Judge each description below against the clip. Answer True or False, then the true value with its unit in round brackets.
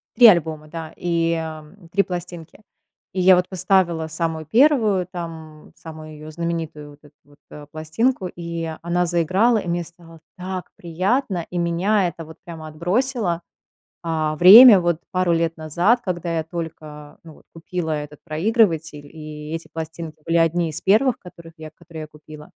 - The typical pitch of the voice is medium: True (170 Hz)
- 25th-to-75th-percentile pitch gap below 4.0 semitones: True (2.4 semitones)